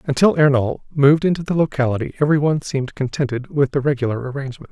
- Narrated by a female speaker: No, male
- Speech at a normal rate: Yes, average, 180 wpm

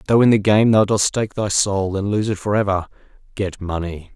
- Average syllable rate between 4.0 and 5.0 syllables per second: No, 5.4 syllables/s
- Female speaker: No, male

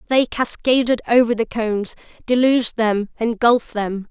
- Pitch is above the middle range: Yes, high, 230 Hz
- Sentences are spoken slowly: Yes, slow, 130 wpm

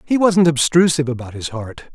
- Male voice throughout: Yes, male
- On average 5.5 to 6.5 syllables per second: Yes, 5.8 syllables/s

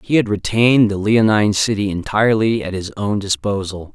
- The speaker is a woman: No, male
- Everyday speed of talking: Yes, average, 165 wpm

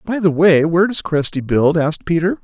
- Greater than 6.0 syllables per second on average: No, 5.7 syllables/s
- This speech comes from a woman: No, male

